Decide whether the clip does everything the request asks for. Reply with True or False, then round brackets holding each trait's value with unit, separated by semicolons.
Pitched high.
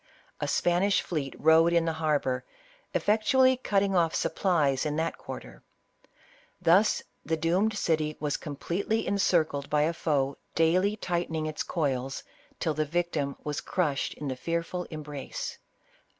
False (165 Hz)